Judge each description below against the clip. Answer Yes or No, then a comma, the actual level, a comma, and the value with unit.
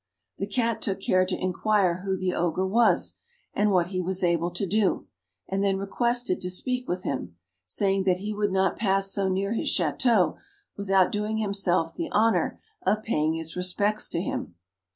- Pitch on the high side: Yes, high, 195 Hz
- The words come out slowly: No, average, 180 wpm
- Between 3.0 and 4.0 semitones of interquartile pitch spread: No, narrow, 2.5 semitones